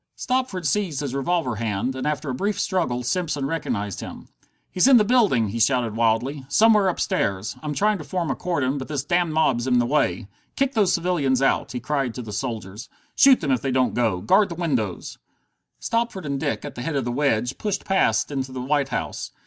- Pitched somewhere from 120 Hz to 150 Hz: Yes, medium, 140 Hz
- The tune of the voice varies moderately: No, wide, 6.5 semitones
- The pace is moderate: No, fast, 210 wpm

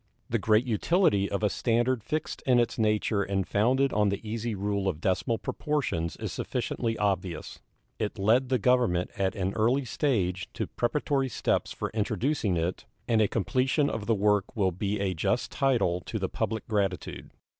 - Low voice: Yes, low, 105 Hz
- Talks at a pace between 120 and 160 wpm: No, average, 175 wpm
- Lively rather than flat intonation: No, average, 3.9 semitones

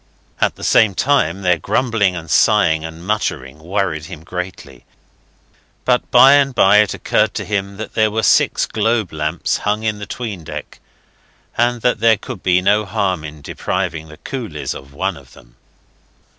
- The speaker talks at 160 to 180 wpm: Yes, average, 170 wpm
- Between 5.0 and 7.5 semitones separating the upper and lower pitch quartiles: Yes, wide, 5.4 semitones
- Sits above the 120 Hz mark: No, low, 100 Hz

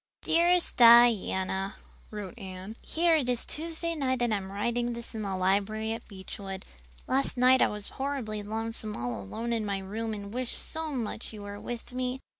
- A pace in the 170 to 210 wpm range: Yes, average, 180 wpm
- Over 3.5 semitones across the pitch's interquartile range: Yes, average, 3.9 semitones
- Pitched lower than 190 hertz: No, high, 225 Hz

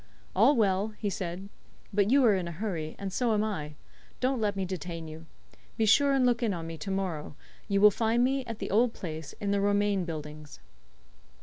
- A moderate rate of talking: No, fast, 210 wpm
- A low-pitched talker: No, high, 200 Hz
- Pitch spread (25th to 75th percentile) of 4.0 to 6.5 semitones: Yes, average, 4.5 semitones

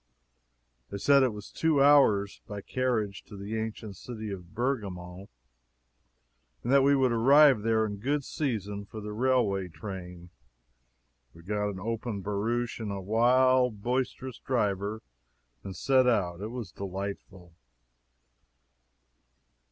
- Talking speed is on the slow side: Yes, slow, 130 wpm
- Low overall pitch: Yes, low, 110 Hz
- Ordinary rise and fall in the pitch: Yes, average, 4.2 semitones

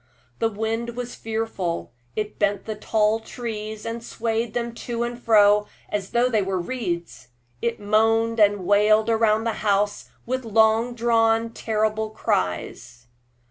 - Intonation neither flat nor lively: No, narrow, 1.7 semitones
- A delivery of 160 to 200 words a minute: No, average, 140 wpm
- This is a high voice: Yes, high, 220 Hz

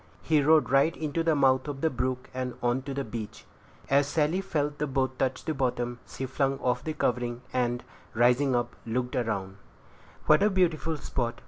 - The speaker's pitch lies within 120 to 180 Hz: Yes, low, 135 Hz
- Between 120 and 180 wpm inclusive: No, average, 195 wpm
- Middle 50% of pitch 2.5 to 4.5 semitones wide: Yes, average, 3.4 semitones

